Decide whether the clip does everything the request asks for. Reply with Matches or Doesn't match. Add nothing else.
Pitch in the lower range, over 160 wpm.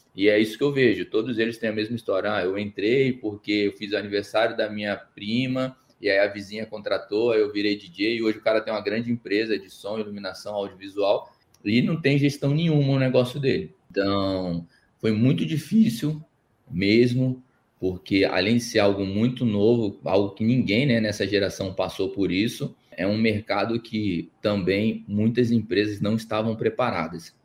Matches